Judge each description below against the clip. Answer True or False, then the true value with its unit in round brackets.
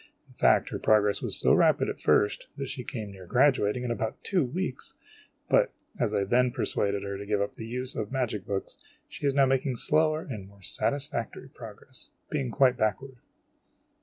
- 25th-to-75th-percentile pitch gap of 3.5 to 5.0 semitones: True (4.5 semitones)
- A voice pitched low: True (125 Hz)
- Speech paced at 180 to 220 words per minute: True (190 wpm)